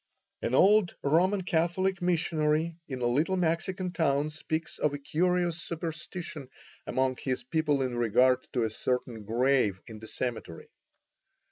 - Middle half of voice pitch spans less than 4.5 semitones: No, average, 5.3 semitones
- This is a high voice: No, medium, 150 Hz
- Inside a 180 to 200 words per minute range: No, average, 140 wpm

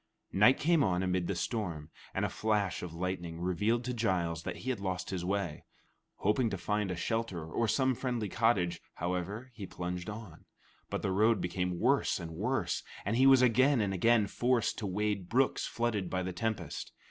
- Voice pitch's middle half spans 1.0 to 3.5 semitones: No, average, 4.5 semitones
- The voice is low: Yes, low, 100 Hz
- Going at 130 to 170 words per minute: No, average, 190 wpm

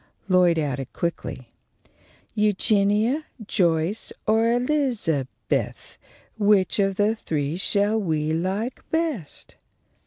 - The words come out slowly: Yes, slow, 90 wpm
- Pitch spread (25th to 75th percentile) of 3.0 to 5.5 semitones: Yes, average, 5.2 semitones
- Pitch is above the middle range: Yes, high, 200 Hz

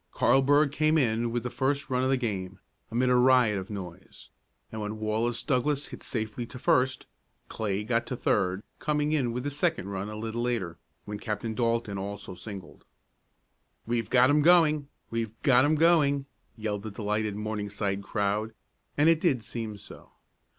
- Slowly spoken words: No, average, 170 wpm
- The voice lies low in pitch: Yes, low, 115 Hz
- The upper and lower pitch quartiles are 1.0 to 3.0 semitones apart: No, average, 4.3 semitones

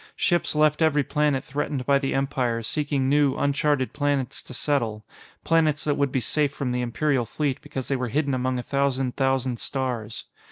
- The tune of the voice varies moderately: No, narrow, 2.3 semitones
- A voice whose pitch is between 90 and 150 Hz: Yes, low, 135 Hz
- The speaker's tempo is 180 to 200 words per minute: Yes, average, 185 wpm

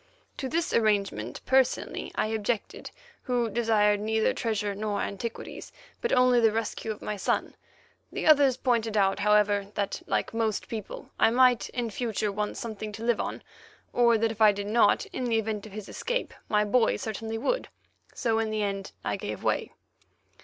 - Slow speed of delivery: No, average, 175 wpm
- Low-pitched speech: No, high, 220 Hz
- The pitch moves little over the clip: Yes, narrow, 2.3 semitones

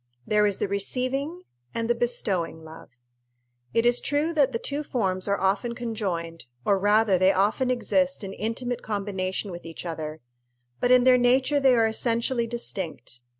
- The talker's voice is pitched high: Yes, high, 225 Hz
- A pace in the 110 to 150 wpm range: No, average, 165 wpm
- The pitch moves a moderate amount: Yes, average, 4.7 semitones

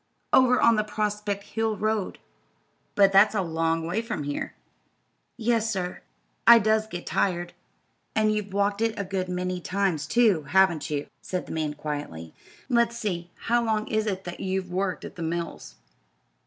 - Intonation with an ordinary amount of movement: Yes, average, 3.8 semitones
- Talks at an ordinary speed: Yes, average, 170 wpm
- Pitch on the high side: Yes, high, 195 Hz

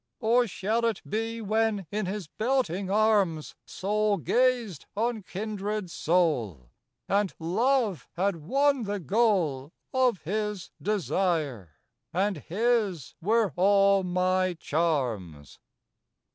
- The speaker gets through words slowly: Yes, slow, 105 wpm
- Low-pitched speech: No, high, 200 Hz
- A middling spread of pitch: Yes, average, 4.4 semitones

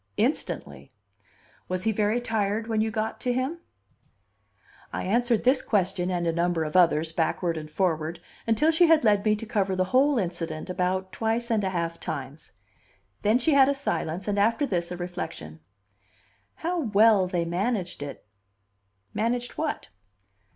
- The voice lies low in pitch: No, high, 200 Hz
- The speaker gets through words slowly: No, average, 160 wpm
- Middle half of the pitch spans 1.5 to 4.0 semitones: No, average, 5.2 semitones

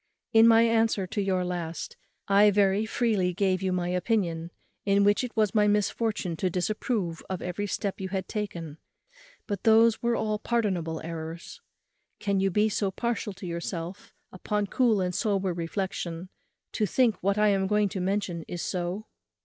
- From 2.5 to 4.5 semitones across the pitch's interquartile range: Yes, average, 2.8 semitones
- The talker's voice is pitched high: Yes, high, 195 Hz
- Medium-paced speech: Yes, average, 170 wpm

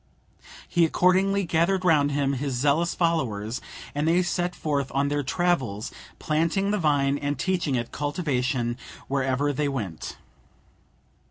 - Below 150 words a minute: Yes, slow, 135 wpm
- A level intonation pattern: No, average, 4.2 semitones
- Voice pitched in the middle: Yes, medium, 145 Hz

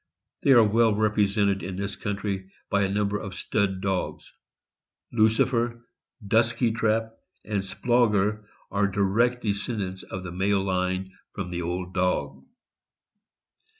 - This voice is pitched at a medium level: No, low, 100 Hz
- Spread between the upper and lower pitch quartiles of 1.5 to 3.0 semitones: Yes, average, 2.7 semitones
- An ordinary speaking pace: No, slow, 125 wpm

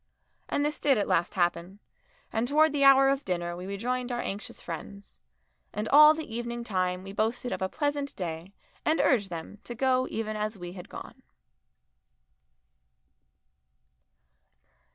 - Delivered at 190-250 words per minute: No, average, 155 wpm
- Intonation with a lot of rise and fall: Yes, wide, 6.4 semitones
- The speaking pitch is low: No, high, 220 Hz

